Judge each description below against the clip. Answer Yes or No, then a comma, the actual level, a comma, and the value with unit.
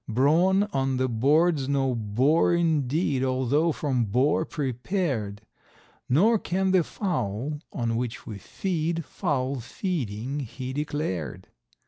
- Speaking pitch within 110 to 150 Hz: Yes, medium, 140 Hz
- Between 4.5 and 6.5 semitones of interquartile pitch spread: Yes, average, 4.9 semitones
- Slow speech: Yes, slow, 115 wpm